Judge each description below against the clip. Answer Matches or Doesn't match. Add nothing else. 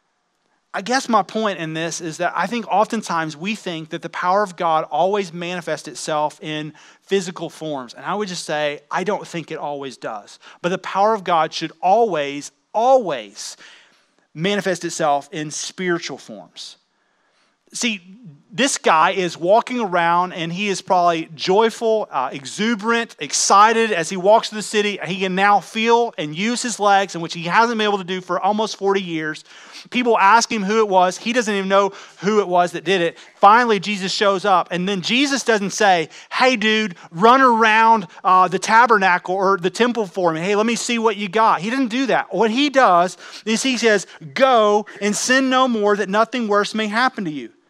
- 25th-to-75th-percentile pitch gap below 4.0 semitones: Doesn't match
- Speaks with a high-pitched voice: Matches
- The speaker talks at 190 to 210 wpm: Matches